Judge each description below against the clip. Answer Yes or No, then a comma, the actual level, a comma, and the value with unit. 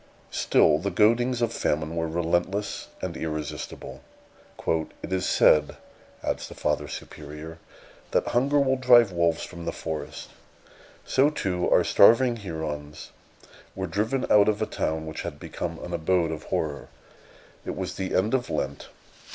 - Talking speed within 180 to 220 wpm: No, average, 150 wpm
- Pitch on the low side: Yes, very low, 90 Hz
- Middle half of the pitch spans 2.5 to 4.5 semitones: No, wide, 5.5 semitones